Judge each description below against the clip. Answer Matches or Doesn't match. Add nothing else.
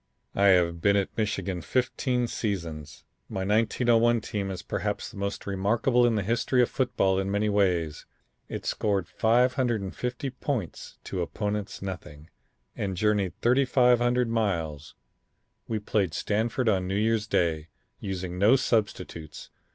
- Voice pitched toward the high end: Doesn't match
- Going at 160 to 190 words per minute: Doesn't match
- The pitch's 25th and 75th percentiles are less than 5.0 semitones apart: Matches